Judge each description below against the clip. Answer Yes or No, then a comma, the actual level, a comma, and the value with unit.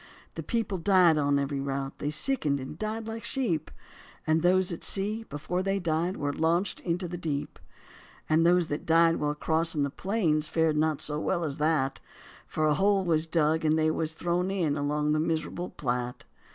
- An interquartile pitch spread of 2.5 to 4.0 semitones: Yes, average, 3.2 semitones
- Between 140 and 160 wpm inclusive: No, average, 185 wpm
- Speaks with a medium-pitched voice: Yes, medium, 160 Hz